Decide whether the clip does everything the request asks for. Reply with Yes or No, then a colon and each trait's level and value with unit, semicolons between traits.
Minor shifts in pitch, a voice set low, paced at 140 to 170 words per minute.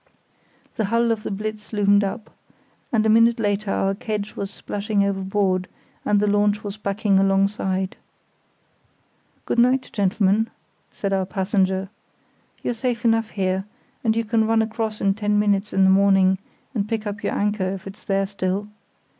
No: narrow, 2.0 semitones; high, 205 Hz; average, 165 wpm